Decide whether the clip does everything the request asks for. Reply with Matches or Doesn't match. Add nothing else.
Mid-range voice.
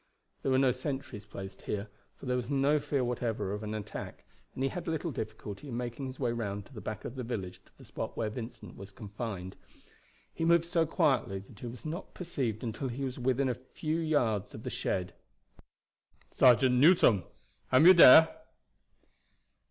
Doesn't match